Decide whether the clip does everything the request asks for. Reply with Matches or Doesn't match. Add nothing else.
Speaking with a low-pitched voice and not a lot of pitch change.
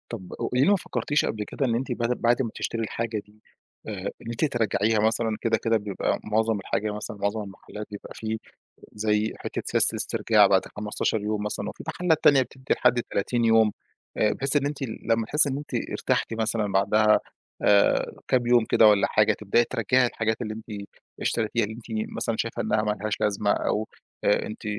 Matches